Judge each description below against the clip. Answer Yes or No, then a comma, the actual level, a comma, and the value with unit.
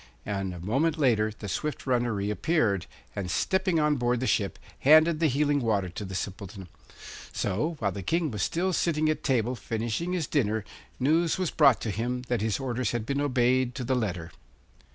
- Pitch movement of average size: No, wide, 6.6 semitones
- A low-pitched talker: Yes, low, 125 Hz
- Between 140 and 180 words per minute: No, average, 190 wpm